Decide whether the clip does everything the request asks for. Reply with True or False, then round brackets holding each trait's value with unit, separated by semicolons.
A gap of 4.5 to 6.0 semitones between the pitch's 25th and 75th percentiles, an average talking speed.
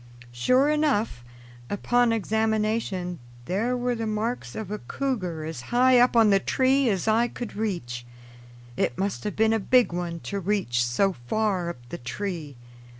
True (5.2 semitones; 160 wpm)